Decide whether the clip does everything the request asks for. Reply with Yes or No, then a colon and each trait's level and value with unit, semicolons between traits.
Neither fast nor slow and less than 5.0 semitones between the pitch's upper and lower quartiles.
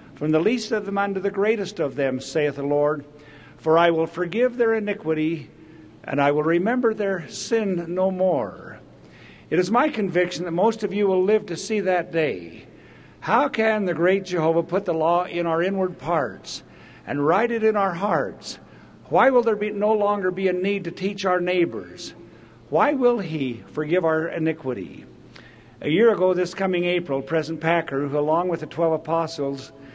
Yes: average, 185 wpm; average, 4.1 semitones